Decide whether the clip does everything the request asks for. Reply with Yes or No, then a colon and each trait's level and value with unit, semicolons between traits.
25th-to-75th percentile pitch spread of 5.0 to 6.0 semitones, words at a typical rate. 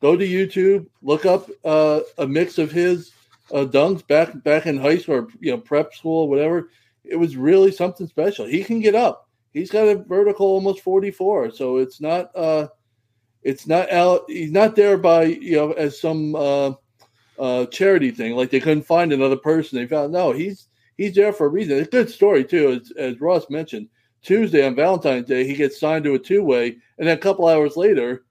No: wide, 5.5 semitones; fast, 210 wpm